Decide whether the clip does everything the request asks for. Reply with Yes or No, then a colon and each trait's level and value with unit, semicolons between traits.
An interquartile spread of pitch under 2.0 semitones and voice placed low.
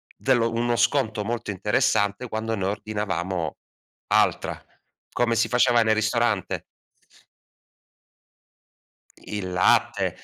No: average, 2.7 semitones; low, 110 Hz